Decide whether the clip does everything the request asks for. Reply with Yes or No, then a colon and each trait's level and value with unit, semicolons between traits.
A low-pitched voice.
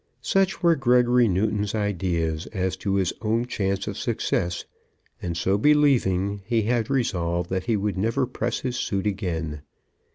Yes: low, 100 Hz